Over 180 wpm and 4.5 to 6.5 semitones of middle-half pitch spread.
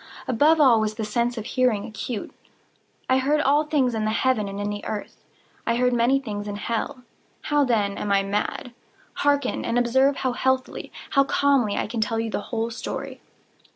No: average, 190 wpm; average, 3.6 semitones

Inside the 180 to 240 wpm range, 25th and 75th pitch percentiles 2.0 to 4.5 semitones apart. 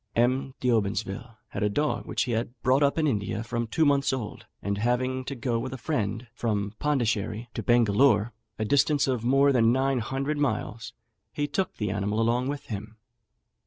Yes: average, 185 wpm; average, 3.7 semitones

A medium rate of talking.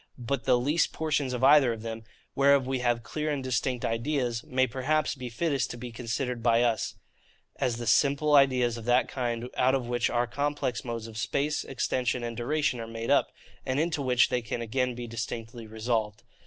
Yes: average, 195 wpm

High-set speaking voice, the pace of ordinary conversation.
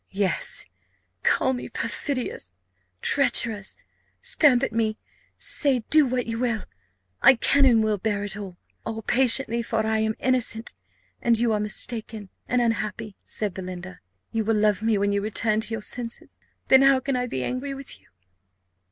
Yes: high, 225 Hz; average, 165 wpm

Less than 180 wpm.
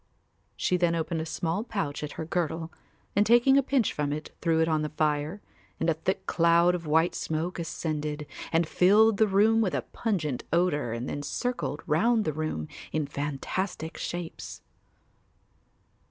Yes: average, 170 wpm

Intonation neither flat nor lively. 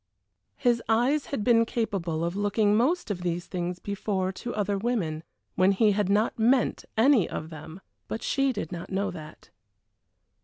Yes: average, 4.3 semitones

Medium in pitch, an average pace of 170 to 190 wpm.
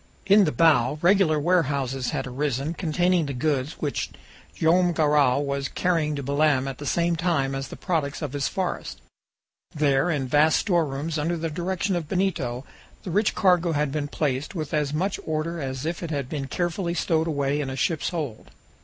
Yes: medium, 155 Hz; average, 185 wpm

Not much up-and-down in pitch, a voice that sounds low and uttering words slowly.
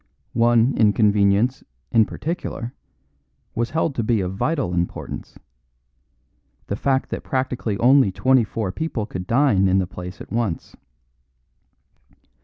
No: average, 4.9 semitones; low, 115 Hz; slow, 125 wpm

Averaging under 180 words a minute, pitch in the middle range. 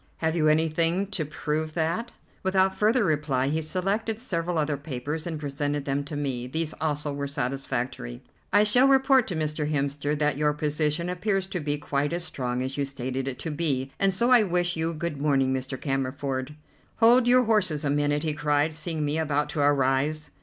No: average, 190 wpm; medium, 150 Hz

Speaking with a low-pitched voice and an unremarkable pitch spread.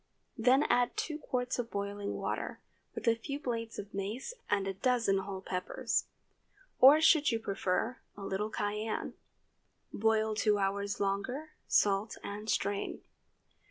No: high, 215 Hz; average, 3.7 semitones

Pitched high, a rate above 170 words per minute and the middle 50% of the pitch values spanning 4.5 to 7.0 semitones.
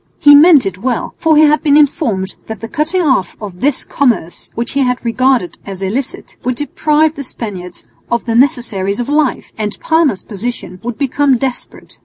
Yes: very high, 250 Hz; average, 180 wpm; wide, 5.6 semitones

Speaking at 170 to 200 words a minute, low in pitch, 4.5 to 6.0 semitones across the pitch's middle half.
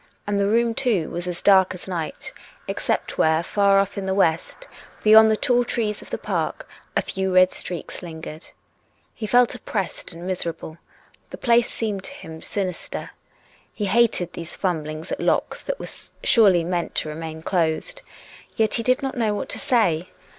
No: average, 175 wpm; high, 190 Hz; average, 4.8 semitones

